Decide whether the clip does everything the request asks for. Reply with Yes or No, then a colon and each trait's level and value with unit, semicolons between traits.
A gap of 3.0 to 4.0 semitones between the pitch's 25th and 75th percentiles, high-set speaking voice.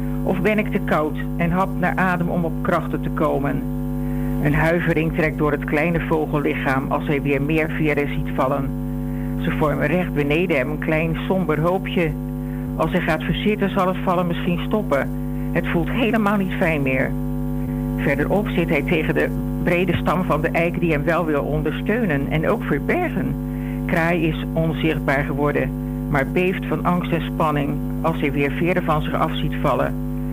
No: average, 3.5 semitones; medium, 140 Hz